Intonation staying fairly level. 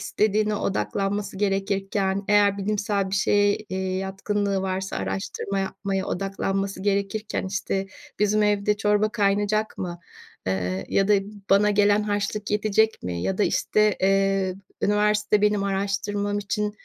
Yes: narrow, 1.3 semitones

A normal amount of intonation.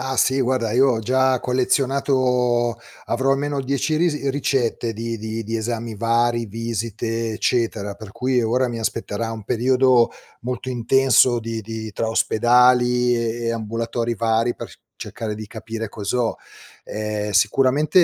No: narrow, 2.2 semitones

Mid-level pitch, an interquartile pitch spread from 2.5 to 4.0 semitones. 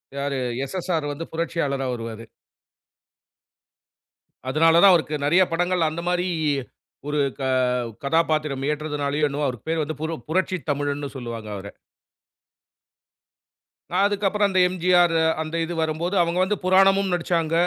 Yes: medium, 160 Hz; average, 3.7 semitones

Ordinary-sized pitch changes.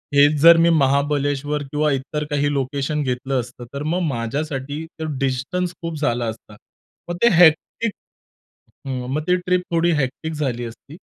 Yes: average, 3.2 semitones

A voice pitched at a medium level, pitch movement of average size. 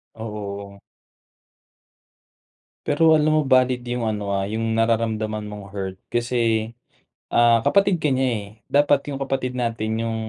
No: low, 115 Hz; average, 3.2 semitones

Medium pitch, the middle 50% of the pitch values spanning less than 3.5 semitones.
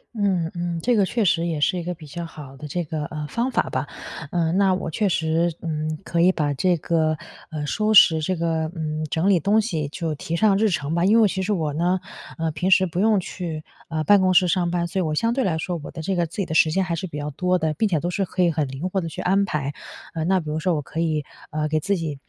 Yes: medium, 170 Hz; average, 3.1 semitones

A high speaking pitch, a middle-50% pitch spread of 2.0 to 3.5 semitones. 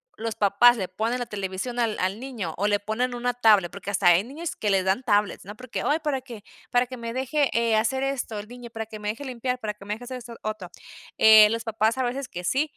Yes: high, 225 Hz; average, 3.2 semitones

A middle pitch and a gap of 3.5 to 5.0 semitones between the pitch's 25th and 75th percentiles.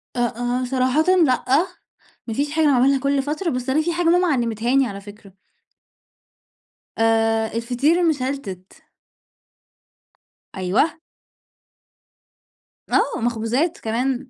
No: very high, 255 Hz; average, 4.2 semitones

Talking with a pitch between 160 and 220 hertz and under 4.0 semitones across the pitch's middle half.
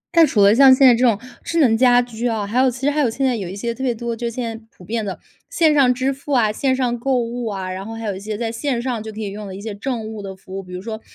No: high, 230 Hz; average, 3.3 semitones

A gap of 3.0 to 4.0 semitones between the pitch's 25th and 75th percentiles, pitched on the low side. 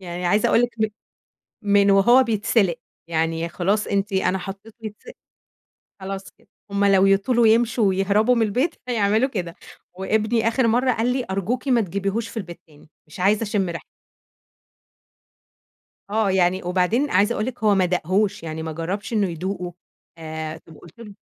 No: average, 3.7 semitones; high, 200 Hz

